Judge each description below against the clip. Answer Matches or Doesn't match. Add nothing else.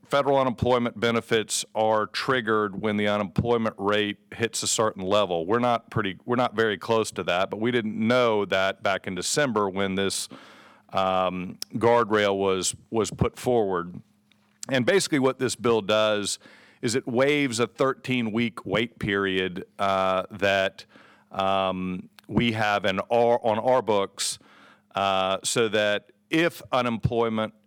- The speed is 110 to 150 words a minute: Matches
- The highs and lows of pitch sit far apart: Doesn't match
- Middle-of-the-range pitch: Doesn't match